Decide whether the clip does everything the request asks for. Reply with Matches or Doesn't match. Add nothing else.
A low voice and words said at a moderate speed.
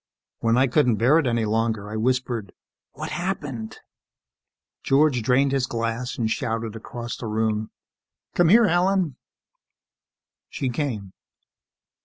Doesn't match